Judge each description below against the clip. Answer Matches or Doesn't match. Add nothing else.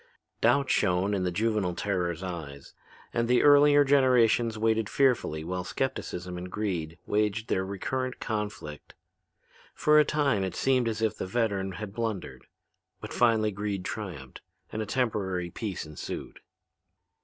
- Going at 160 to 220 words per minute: Doesn't match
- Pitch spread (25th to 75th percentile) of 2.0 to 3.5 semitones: Doesn't match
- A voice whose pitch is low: Matches